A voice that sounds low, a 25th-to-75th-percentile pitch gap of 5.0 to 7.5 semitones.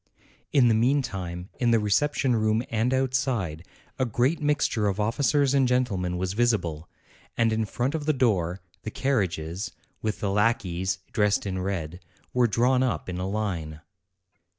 Yes: low, 110 Hz; average, 5.3 semitones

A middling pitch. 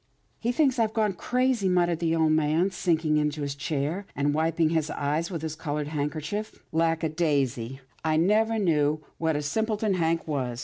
Yes: medium, 160 Hz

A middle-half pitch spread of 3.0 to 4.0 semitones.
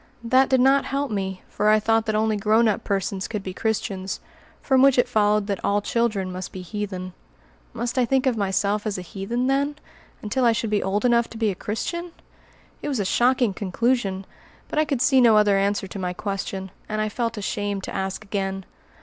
Yes: average, 3.6 semitones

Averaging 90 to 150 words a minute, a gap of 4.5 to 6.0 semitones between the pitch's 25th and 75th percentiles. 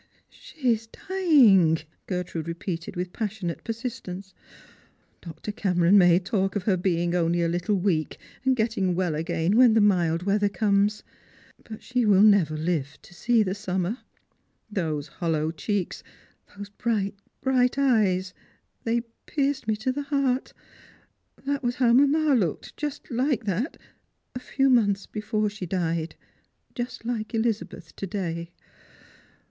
Yes: average, 145 wpm; average, 5.2 semitones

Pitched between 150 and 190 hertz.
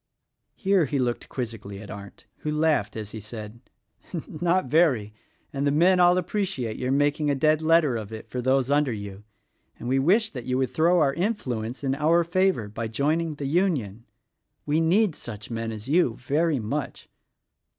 No: medium, 140 Hz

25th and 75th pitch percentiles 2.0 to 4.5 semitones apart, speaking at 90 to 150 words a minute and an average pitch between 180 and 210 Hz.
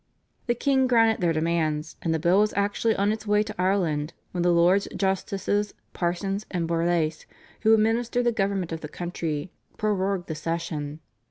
No: average, 4.1 semitones; average, 170 wpm; medium, 185 Hz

